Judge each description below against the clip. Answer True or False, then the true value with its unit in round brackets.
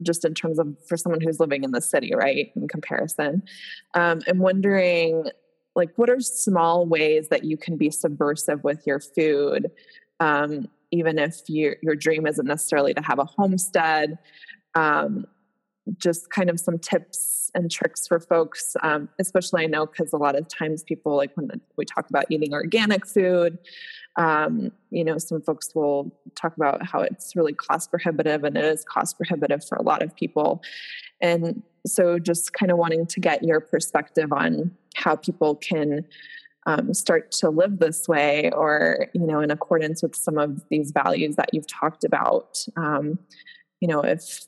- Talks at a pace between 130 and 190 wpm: True (175 wpm)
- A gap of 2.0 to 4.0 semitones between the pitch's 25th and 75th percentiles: True (3.1 semitones)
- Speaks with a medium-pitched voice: True (165 Hz)